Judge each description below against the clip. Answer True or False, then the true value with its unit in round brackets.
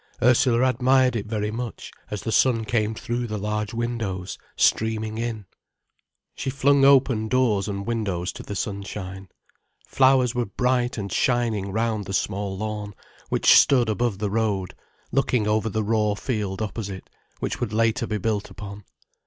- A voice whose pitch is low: True (110 Hz)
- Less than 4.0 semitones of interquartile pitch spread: True (2.8 semitones)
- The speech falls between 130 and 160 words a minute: True (155 wpm)